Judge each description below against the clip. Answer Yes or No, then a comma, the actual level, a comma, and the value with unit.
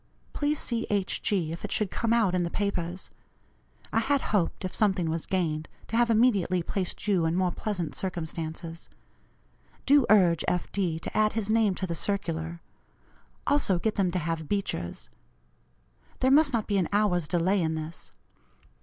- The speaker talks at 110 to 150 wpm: No, average, 170 wpm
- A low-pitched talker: No, medium, 185 Hz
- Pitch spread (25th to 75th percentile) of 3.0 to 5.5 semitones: Yes, average, 4.1 semitones